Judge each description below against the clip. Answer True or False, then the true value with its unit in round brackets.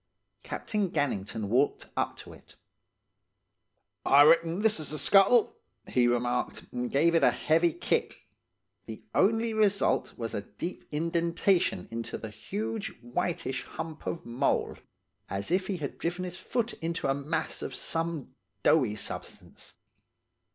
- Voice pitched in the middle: True (165 Hz)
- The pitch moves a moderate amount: False (6.7 semitones)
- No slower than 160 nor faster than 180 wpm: False (135 wpm)